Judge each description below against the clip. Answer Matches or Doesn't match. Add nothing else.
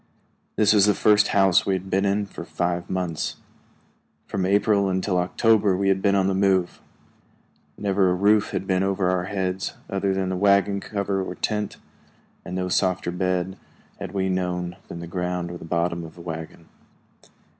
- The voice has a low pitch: Matches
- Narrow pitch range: Matches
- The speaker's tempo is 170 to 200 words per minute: Matches